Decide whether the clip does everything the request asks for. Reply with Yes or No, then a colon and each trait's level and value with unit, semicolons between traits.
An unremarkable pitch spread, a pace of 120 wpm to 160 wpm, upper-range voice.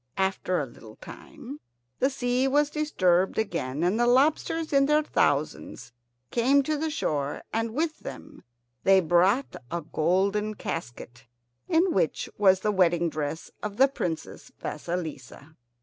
No: wide, 8.7 semitones; average, 140 wpm; high, 195 Hz